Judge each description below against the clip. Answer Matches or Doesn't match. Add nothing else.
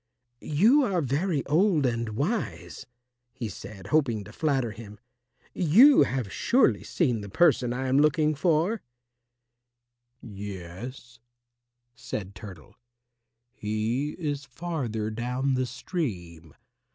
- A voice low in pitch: Matches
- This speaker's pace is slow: Matches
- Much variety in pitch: Matches